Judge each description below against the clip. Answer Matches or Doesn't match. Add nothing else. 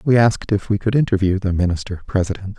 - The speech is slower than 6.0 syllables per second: Doesn't match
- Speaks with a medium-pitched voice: Doesn't match